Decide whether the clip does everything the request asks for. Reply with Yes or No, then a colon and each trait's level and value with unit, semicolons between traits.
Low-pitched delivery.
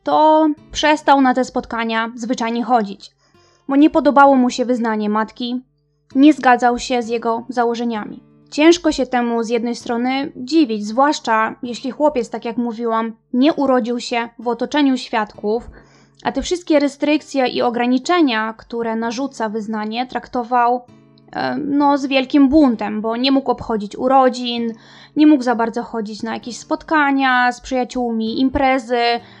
No: high, 245 Hz